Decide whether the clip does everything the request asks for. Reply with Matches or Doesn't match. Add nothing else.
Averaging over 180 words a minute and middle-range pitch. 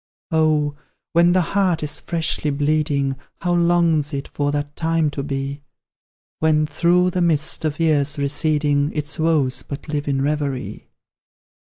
Doesn't match